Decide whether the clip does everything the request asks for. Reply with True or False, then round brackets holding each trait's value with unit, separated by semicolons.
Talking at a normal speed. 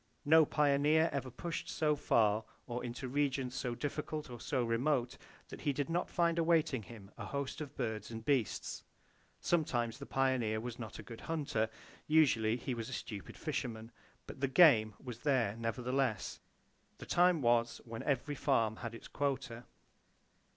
True (165 wpm)